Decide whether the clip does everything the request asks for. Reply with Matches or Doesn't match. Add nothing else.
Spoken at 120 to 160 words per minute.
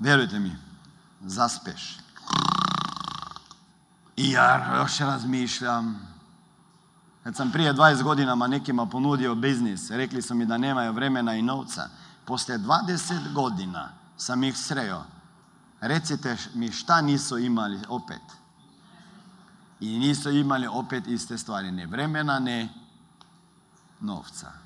Doesn't match